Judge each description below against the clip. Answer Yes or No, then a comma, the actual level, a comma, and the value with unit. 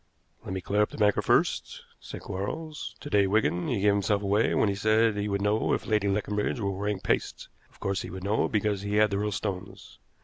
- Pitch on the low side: Yes, low, 105 Hz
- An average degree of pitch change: No, narrow, 1.3 semitones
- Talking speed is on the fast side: Yes, fast, 230 wpm